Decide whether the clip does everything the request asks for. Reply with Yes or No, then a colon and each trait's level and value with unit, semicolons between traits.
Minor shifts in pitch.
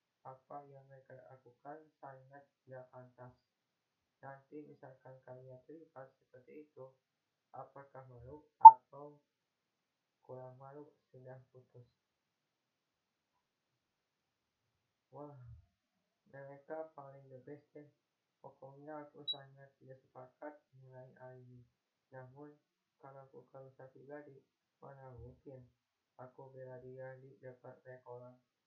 Yes: narrow, 1.8 semitones